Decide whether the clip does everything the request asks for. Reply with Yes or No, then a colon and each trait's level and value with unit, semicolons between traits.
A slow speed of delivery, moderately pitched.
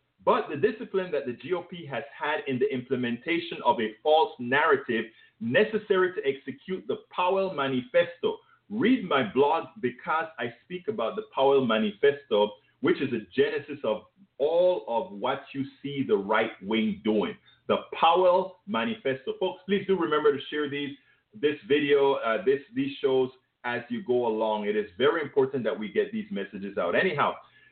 No: average, 165 wpm; medium, 180 Hz